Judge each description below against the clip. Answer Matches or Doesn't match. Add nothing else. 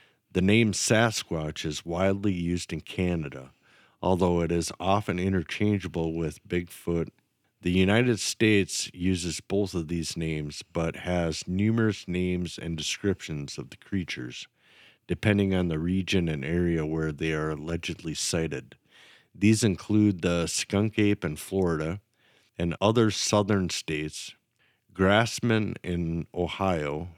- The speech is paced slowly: Matches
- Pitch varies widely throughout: Doesn't match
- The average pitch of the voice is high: Doesn't match